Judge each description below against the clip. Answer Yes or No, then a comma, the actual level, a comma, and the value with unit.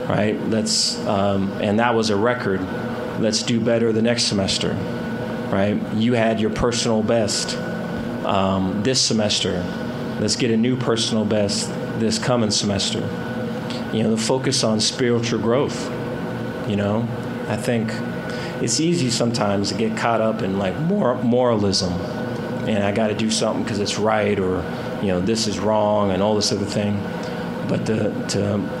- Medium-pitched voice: No, low, 110 Hz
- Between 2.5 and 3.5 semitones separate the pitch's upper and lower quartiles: Yes, average, 2.8 semitones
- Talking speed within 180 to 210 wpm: No, average, 160 wpm